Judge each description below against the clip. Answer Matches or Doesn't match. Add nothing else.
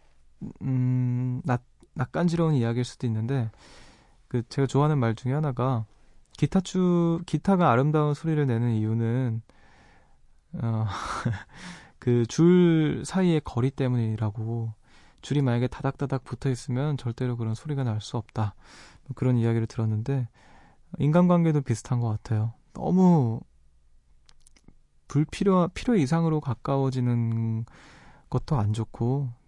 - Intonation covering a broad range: Doesn't match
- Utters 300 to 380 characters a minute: Doesn't match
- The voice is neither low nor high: Doesn't match